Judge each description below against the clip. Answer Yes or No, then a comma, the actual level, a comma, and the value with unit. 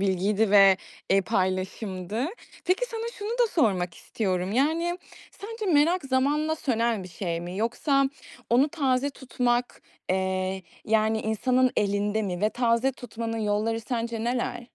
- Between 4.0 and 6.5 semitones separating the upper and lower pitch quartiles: Yes, average, 5.3 semitones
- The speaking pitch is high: Yes, high, 230 Hz